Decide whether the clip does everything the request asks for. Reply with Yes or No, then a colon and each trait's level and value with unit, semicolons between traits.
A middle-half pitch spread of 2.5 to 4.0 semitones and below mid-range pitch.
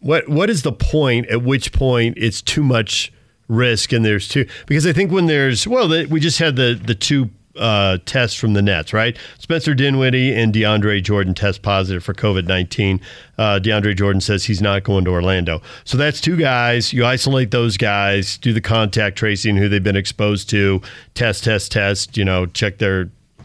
No: average, 4.4 semitones; low, 110 Hz